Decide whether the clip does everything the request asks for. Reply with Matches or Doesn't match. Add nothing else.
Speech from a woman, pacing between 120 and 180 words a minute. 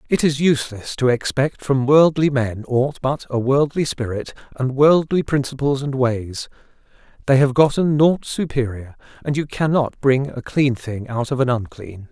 Doesn't match